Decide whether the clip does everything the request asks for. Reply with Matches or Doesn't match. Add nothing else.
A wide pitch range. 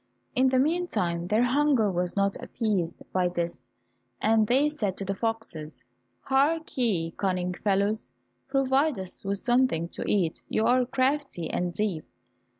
Matches